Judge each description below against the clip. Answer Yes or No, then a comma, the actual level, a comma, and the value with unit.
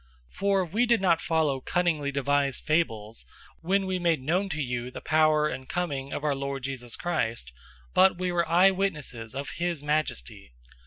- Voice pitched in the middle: Yes, medium, 155 Hz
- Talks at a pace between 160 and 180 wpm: Yes, average, 170 wpm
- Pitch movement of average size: Yes, average, 4.6 semitones